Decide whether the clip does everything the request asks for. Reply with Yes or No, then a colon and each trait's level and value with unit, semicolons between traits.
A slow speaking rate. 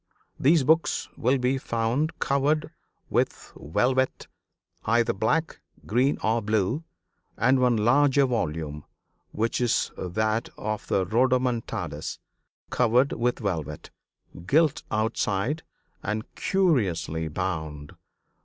Yes: slow, 100 wpm